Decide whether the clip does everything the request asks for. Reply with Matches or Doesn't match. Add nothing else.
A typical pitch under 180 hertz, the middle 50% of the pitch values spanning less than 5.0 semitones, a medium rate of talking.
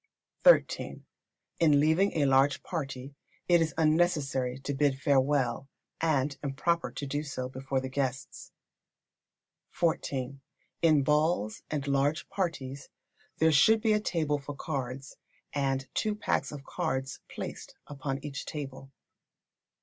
Doesn't match